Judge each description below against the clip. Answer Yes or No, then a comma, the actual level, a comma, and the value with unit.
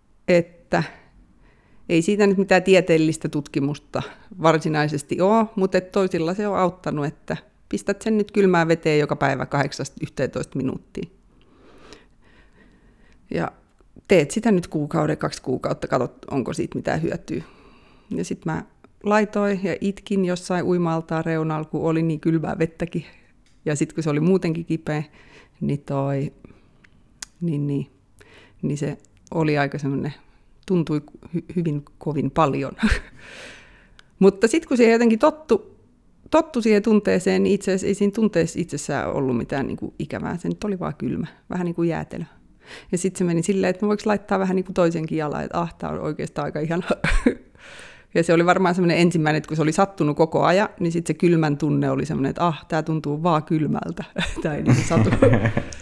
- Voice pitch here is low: No, medium, 165 Hz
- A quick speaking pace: Yes, fast, 160 wpm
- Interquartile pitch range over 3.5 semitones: Yes, average, 4.2 semitones